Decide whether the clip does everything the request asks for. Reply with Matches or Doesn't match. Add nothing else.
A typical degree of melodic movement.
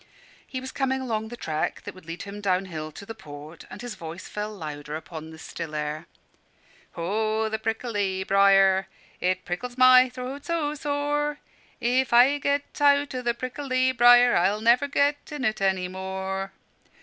Doesn't match